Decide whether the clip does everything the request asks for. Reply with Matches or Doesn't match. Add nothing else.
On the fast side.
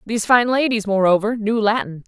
Doesn't match